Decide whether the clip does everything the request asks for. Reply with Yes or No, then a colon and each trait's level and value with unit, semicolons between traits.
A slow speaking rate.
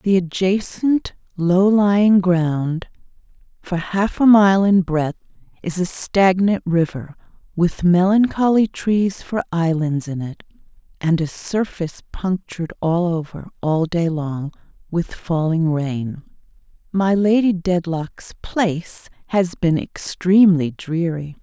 Yes: slow, 120 wpm